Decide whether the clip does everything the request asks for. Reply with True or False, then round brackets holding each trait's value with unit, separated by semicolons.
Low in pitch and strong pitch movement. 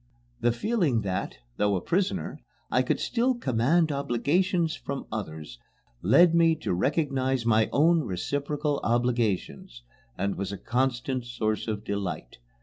True (125 Hz; 6.8 semitones)